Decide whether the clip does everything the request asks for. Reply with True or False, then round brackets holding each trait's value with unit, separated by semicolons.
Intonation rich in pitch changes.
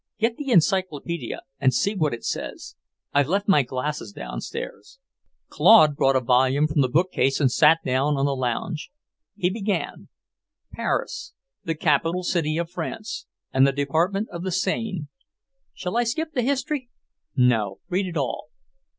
True (6.5 semitones)